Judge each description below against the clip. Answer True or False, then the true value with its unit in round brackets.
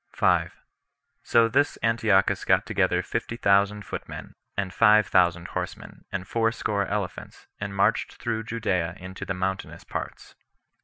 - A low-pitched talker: True (100 Hz)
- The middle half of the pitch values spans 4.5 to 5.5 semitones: False (3.1 semitones)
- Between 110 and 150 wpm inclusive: True (135 wpm)